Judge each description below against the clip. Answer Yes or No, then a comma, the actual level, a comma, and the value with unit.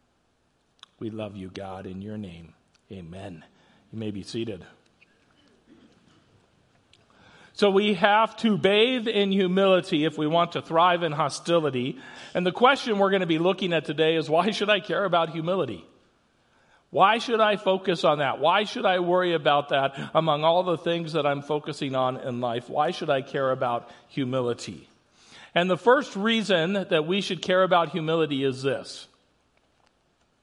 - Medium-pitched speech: Yes, medium, 165 Hz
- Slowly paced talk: No, average, 165 wpm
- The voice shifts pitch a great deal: Yes, wide, 6.1 semitones